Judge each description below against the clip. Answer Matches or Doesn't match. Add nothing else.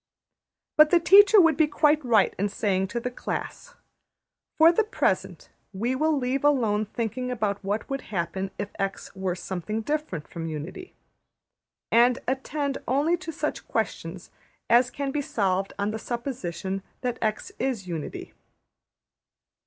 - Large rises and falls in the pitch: Matches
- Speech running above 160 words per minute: Doesn't match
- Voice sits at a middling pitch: Doesn't match